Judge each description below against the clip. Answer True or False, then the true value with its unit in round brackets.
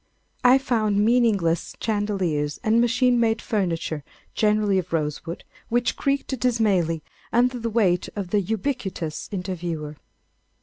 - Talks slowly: True (120 wpm)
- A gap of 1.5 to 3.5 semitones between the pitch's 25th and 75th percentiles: False (5.2 semitones)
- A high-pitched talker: True (205 Hz)